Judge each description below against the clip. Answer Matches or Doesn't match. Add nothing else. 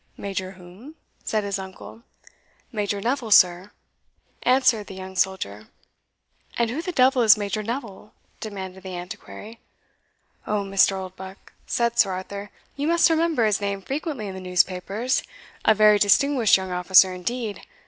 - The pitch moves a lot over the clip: Doesn't match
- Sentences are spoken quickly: Doesn't match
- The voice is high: Matches